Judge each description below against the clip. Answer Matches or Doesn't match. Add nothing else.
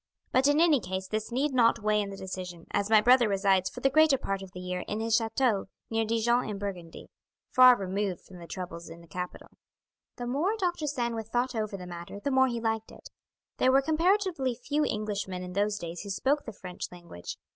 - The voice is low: Doesn't match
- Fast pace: Matches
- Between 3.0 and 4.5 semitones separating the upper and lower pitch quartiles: Doesn't match